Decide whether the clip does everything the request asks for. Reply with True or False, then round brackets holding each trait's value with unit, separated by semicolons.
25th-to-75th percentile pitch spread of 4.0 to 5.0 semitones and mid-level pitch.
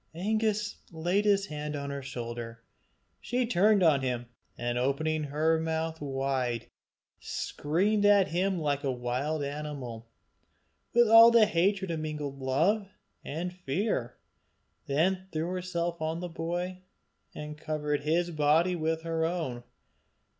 True (4.5 semitones; 160 Hz)